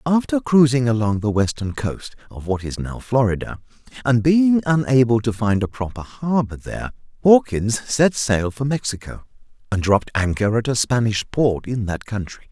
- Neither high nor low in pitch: No, low, 120 Hz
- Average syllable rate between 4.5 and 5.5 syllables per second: Yes, 4.9 syllables/s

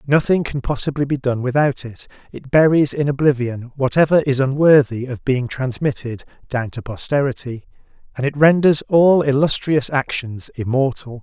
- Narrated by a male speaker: Yes, male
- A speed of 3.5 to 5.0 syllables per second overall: Yes, 4.9 syllables/s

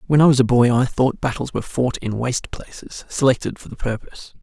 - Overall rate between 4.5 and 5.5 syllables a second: No, 6.0 syllables/s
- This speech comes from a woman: No, male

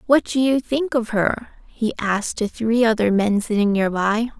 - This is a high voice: Yes, high, 225 Hz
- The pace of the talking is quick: No, average, 190 wpm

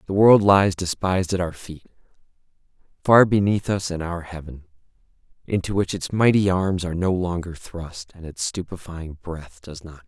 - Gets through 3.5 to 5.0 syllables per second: Yes, 4.9 syllables/s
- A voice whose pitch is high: No, very low, 90 Hz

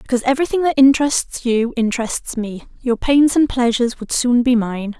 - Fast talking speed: No, average, 180 wpm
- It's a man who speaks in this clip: No, female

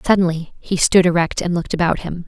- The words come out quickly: Yes, fast, 210 wpm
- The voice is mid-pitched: Yes, medium, 175 Hz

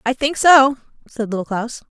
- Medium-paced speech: Yes, average, 185 wpm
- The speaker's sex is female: Yes, female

